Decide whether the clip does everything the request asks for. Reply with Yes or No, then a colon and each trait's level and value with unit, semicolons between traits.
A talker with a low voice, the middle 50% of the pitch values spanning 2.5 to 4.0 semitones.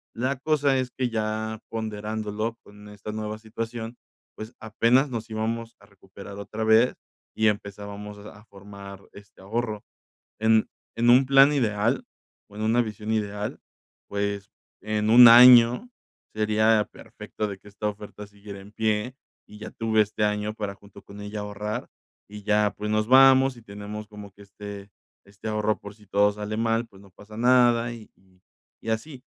No: low, 110 Hz; narrow, 1.9 semitones